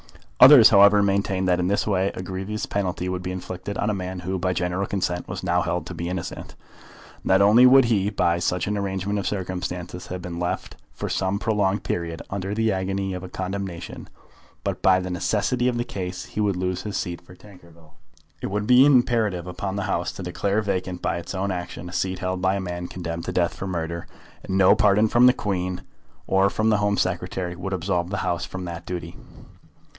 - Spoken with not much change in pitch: Yes, narrow, 2.1 semitones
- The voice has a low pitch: Yes, very low, 95 Hz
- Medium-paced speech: No, fast, 210 wpm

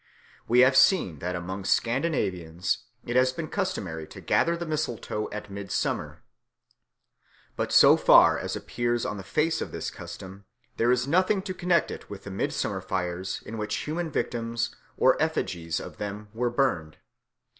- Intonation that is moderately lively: No, wide, 7.9 semitones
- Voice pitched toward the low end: Yes, low, 115 Hz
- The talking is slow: No, average, 160 wpm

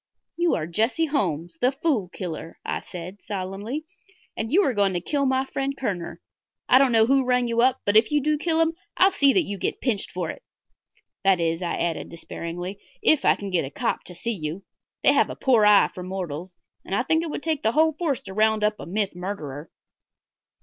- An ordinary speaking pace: No, fast, 220 wpm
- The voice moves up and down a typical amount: No, wide, 7.2 semitones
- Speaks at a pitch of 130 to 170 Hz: No, high, 215 Hz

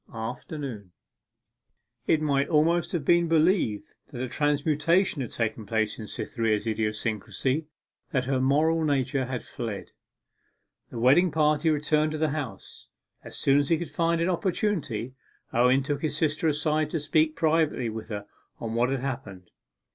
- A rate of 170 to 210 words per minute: No, average, 155 wpm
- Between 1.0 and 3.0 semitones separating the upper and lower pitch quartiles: No, average, 4.8 semitones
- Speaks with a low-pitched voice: No, medium, 145 Hz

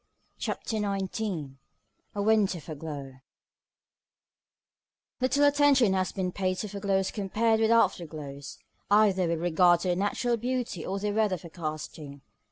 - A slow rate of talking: Yes, slow, 125 wpm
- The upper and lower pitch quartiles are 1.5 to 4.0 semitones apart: No, average, 4.6 semitones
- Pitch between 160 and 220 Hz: Yes, high, 190 Hz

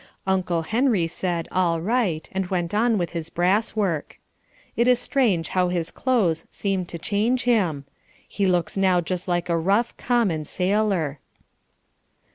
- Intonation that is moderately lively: Yes, average, 4.2 semitones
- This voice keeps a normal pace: Yes, average, 150 wpm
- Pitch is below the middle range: No, medium, 185 Hz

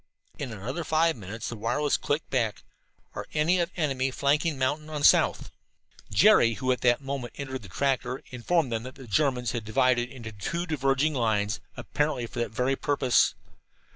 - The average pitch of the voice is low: Yes, low, 130 Hz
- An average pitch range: Yes, average, 3.7 semitones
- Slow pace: No, average, 170 wpm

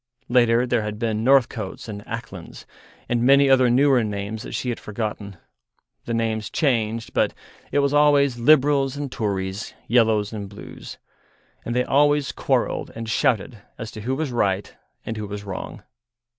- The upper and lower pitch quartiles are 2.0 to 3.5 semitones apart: No, average, 3.9 semitones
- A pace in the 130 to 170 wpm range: Yes, average, 160 wpm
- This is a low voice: Yes, low, 115 Hz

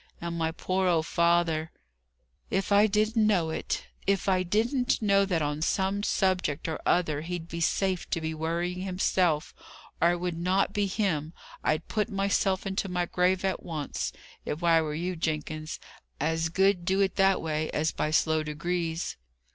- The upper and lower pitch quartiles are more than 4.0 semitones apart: No, average, 3.2 semitones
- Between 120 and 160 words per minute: No, average, 175 wpm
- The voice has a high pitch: No, medium, 175 Hz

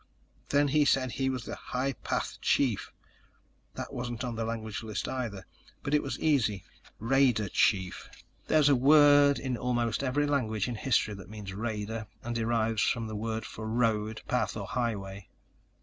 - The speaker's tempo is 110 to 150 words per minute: No, average, 165 wpm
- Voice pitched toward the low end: Yes, low, 115 Hz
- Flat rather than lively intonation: No, average, 3.5 semitones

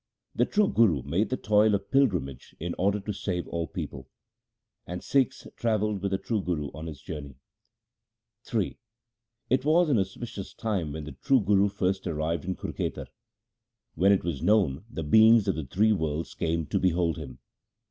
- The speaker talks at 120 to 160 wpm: No, average, 175 wpm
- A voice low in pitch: Yes, very low, 95 Hz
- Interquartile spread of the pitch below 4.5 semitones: No, average, 4.9 semitones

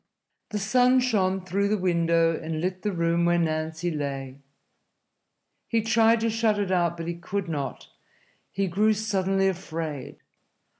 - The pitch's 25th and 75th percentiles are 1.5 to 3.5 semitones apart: No, average, 4.0 semitones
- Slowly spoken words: No, average, 150 wpm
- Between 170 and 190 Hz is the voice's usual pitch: Yes, medium, 185 Hz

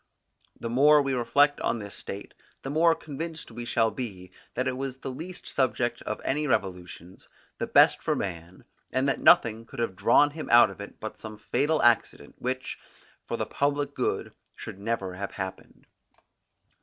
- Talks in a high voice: No, low, 120 Hz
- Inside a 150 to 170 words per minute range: No, average, 180 wpm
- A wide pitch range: Yes, wide, 5.7 semitones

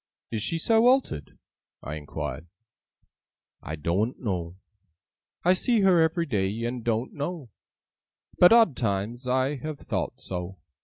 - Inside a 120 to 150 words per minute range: Yes, slow, 135 wpm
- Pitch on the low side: Yes, low, 120 Hz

